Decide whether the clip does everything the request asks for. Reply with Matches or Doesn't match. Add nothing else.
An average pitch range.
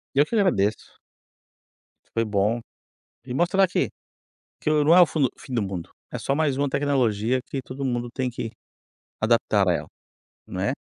Matches